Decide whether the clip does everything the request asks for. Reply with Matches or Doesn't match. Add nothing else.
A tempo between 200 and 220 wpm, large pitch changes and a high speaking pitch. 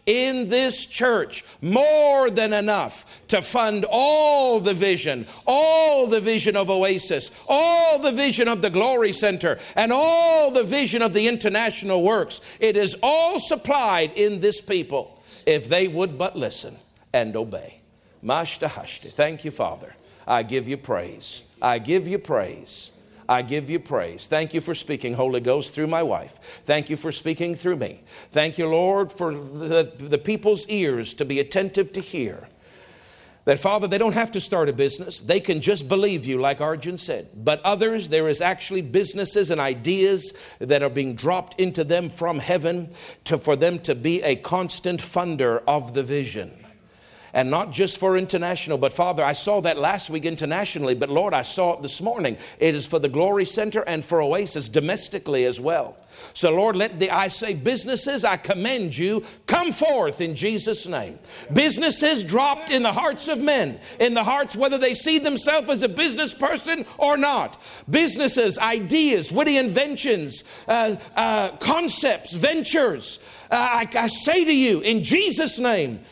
Doesn't match